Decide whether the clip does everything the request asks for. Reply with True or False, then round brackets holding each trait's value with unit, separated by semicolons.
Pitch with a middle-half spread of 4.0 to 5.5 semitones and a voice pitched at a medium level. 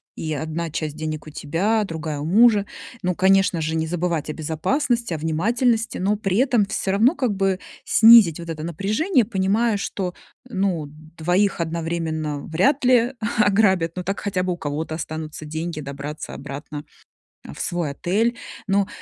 True (4.7 semitones; 175 Hz)